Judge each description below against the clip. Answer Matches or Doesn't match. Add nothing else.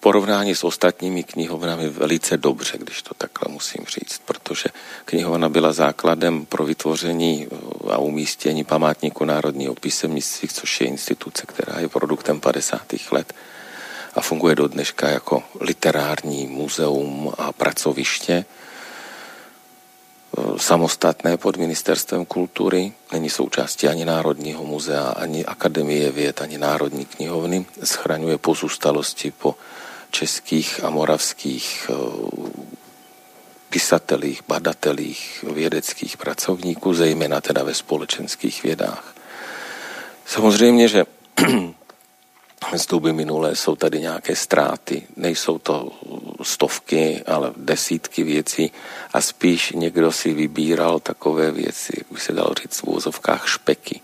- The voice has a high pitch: Doesn't match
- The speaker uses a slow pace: Matches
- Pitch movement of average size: Doesn't match